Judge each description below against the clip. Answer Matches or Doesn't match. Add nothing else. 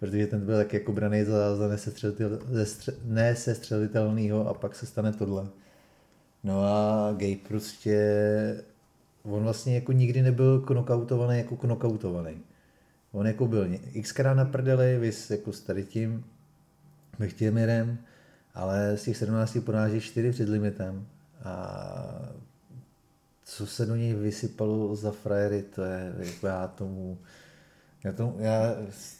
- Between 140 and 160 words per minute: Doesn't match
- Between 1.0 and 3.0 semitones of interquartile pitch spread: Matches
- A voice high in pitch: Doesn't match